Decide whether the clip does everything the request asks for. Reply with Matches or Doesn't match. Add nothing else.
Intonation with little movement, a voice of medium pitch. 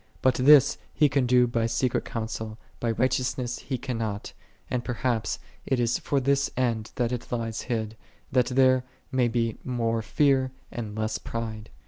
Doesn't match